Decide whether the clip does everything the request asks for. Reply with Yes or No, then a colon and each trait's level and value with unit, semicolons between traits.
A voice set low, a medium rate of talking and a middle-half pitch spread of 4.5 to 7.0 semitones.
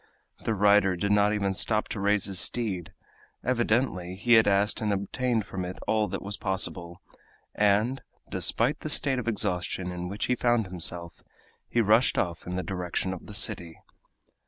No: low, 100 Hz; average, 175 wpm; average, 3.5 semitones